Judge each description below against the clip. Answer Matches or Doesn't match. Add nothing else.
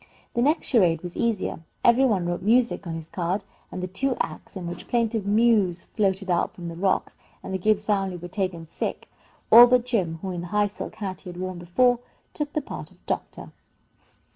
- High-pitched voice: Matches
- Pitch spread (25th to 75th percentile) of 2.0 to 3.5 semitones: Doesn't match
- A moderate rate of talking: Doesn't match